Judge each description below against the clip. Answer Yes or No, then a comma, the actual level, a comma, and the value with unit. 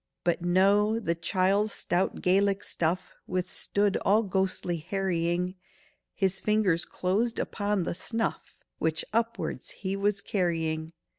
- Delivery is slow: Yes, slow, 115 wpm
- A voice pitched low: No, high, 190 Hz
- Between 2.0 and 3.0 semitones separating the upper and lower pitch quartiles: Yes, average, 2.7 semitones